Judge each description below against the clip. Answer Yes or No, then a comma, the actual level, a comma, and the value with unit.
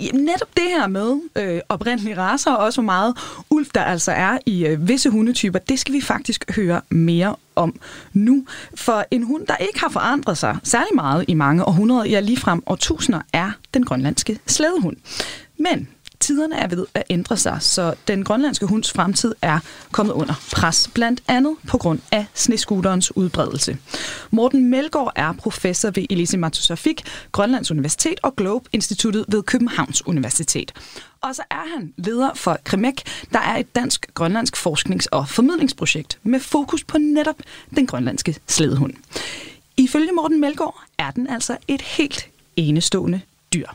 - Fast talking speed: No, average, 155 wpm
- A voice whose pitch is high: Yes, high, 225 Hz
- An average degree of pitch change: No, wide, 6.7 semitones